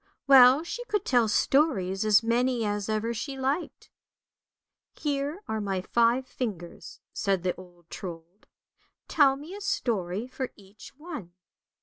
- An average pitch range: No, wide, 6.1 semitones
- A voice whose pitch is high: Yes, high, 235 Hz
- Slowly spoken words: No, average, 145 wpm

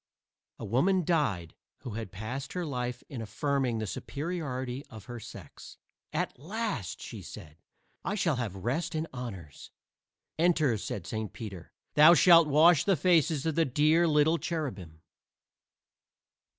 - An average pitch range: No, wide, 6.7 semitones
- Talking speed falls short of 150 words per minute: Yes, average, 140 wpm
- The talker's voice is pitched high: No, medium, 140 Hz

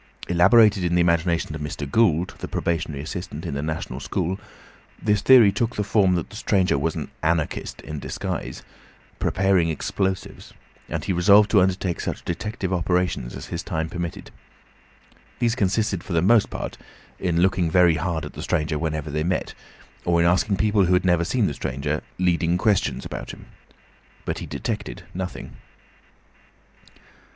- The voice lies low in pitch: Yes, very low, 90 Hz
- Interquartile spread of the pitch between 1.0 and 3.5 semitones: Yes, average, 3.1 semitones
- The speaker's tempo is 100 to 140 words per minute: No, average, 165 wpm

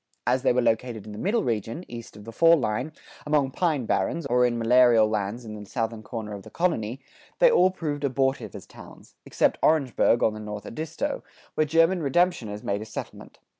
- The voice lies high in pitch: No, low, 125 Hz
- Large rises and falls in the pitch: Yes, wide, 5.9 semitones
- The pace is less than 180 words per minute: No, average, 200 wpm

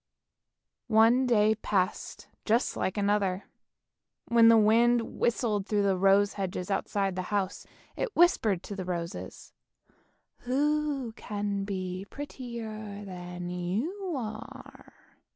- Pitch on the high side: Yes, high, 210 Hz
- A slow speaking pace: Yes, slow, 115 wpm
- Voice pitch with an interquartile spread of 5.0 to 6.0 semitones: No, average, 3.5 semitones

